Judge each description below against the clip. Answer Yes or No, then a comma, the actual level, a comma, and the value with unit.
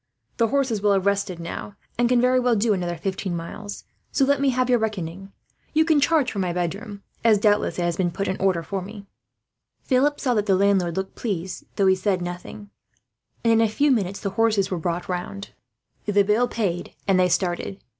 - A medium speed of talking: No, fast, 210 wpm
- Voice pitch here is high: Yes, high, 200 Hz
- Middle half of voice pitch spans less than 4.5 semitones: Yes, average, 3.8 semitones